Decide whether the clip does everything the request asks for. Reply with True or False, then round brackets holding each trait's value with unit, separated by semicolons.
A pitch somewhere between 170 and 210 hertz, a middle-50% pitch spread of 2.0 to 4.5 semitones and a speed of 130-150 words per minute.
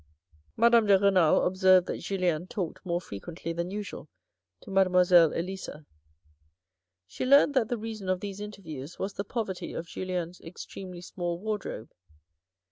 True (185 Hz; 2.8 semitones; 145 wpm)